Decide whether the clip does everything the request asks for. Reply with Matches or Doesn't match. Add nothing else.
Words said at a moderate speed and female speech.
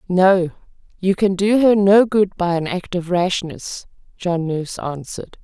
Matches